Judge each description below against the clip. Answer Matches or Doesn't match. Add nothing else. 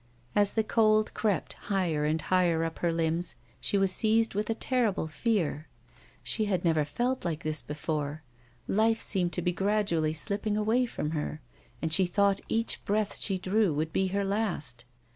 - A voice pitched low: Doesn't match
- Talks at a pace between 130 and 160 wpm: Doesn't match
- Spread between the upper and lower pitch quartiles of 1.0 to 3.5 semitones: Doesn't match